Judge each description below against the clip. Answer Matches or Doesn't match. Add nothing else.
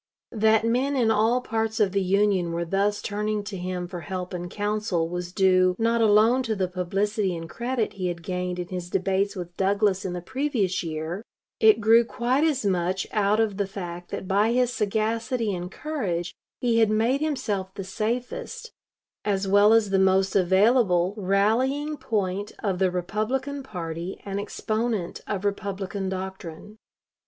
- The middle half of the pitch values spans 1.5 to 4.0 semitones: Matches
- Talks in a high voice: Matches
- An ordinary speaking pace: Matches